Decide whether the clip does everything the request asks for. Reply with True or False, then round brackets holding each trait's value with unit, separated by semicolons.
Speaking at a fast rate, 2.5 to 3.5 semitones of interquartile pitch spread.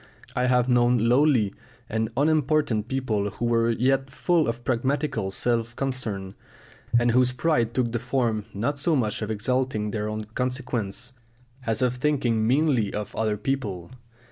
False (150 wpm; 3.2 semitones)